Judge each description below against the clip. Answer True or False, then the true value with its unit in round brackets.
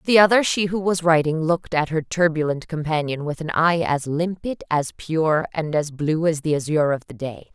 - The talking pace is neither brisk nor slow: False (215 wpm)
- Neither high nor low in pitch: True (160 Hz)